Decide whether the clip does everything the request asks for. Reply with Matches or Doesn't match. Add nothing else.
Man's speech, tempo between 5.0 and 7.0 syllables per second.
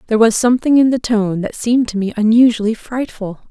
Doesn't match